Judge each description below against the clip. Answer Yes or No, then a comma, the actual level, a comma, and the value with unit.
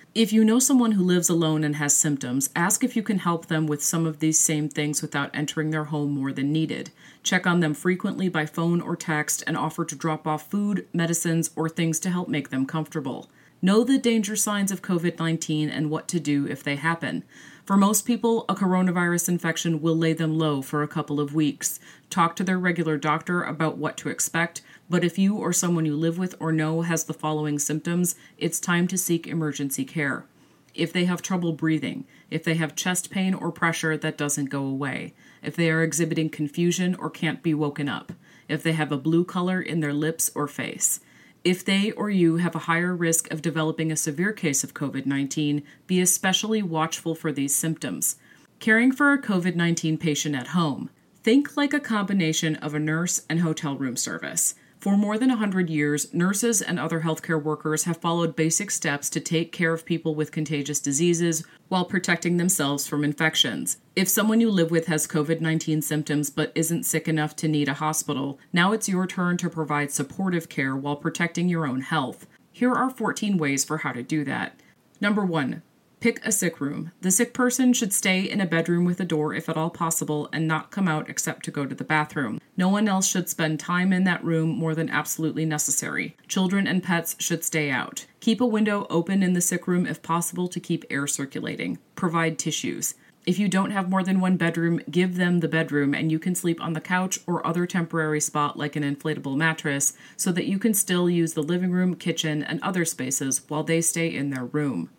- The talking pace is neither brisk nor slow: No, fast, 210 wpm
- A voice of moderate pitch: Yes, medium, 165 Hz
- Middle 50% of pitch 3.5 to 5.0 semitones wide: No, average, 3.0 semitones